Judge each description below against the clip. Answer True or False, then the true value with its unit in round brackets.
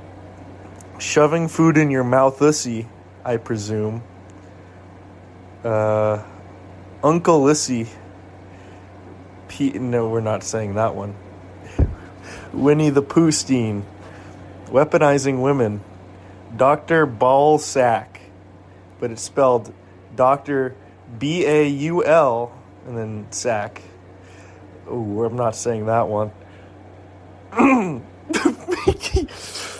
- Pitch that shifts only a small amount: False (5.3 semitones)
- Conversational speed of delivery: False (80 wpm)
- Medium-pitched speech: False (105 Hz)